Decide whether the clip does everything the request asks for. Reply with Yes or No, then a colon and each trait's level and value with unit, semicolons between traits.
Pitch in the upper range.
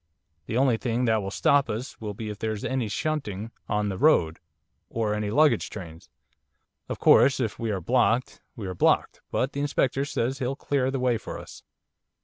No: low, 115 Hz